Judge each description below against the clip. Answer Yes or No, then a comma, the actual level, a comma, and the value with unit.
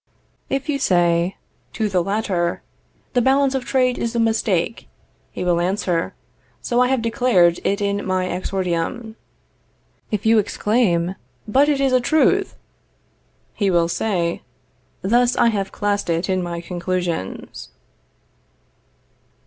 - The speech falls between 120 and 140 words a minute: Yes, slow, 135 wpm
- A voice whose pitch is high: Yes, high, 200 Hz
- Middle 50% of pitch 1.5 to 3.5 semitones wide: No, wide, 5.4 semitones